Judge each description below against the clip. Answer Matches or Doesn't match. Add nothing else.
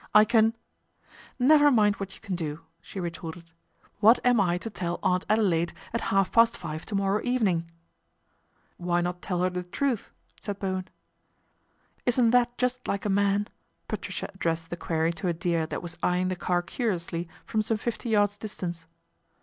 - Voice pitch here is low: Doesn't match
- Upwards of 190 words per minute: Matches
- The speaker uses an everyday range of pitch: Matches